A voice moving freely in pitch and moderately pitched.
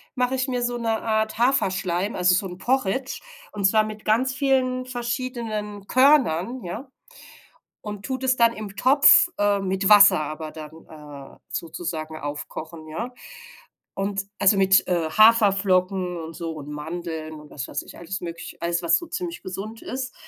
No: wide, 6.1 semitones; high, 200 Hz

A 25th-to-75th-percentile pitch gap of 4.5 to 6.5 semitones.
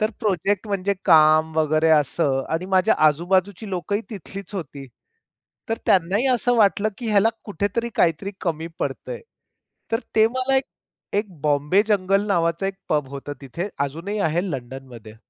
Yes: average, 4.9 semitones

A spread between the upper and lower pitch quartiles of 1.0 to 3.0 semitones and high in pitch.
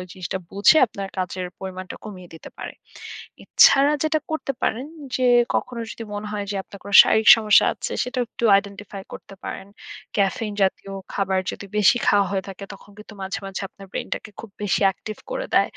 Yes: narrow, 2.4 semitones; high, 200 Hz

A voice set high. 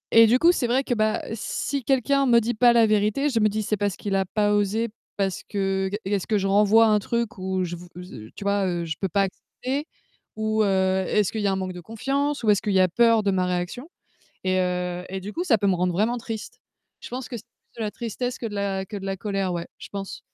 Yes: high, 205 Hz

